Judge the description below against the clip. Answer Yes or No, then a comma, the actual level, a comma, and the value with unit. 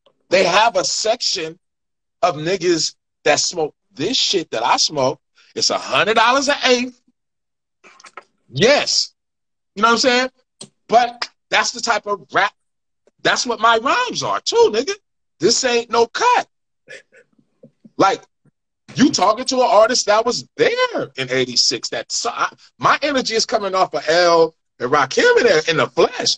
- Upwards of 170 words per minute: No, average, 150 wpm